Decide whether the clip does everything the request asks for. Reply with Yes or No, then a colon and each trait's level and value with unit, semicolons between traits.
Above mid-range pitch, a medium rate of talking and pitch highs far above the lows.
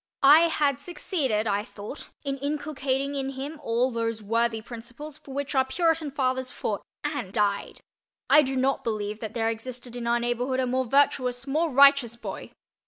No: very high, 260 Hz; average, 170 wpm; average, 3.4 semitones